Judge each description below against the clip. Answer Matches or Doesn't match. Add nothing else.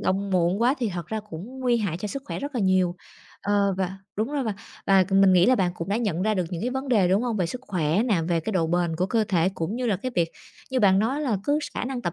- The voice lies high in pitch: Matches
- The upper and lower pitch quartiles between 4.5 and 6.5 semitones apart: Matches